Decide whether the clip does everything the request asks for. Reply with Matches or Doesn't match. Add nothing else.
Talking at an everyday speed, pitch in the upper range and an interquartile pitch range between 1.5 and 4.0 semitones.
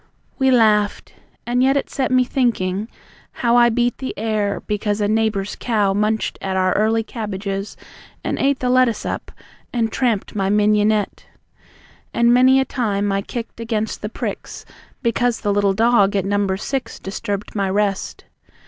Matches